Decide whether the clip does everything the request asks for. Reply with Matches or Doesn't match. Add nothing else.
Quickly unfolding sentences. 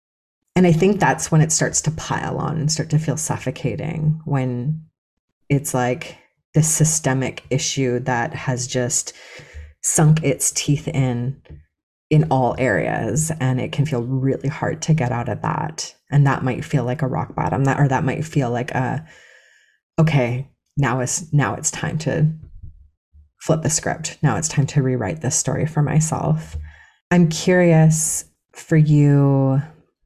Doesn't match